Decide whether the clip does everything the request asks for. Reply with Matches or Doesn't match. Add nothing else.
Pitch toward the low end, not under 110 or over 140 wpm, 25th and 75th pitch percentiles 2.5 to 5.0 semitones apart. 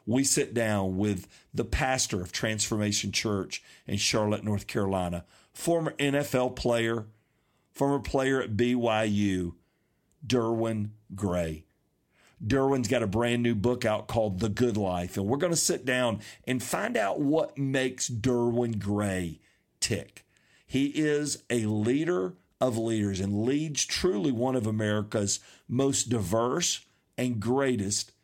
Matches